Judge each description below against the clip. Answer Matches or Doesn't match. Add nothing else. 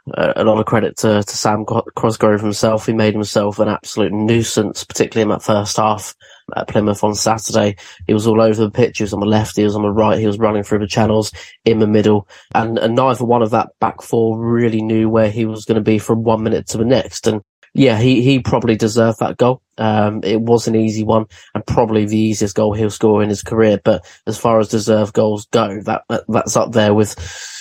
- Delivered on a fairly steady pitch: Matches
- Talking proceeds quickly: Matches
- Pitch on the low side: Matches